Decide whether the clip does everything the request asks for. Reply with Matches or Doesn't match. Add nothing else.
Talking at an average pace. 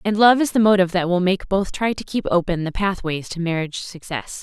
Doesn't match